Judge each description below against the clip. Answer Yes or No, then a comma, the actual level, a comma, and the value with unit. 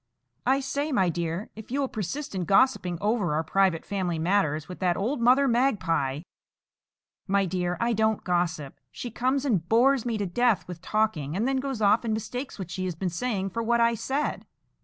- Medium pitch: No, high, 205 Hz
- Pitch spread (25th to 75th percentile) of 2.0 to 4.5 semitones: No, wide, 5.4 semitones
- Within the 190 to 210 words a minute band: Yes, average, 200 wpm